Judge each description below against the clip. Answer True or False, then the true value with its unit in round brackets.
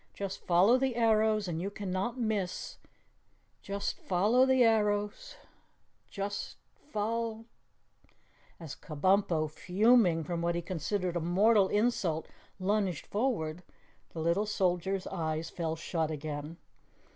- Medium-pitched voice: False (195 Hz)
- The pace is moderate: False (120 wpm)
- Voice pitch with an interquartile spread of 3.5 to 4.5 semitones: True (4.1 semitones)